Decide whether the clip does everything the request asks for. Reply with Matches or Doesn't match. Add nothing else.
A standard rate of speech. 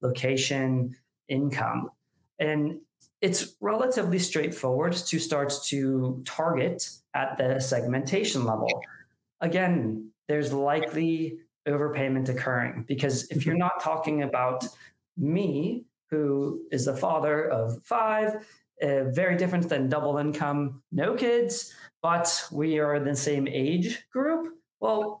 Doesn't match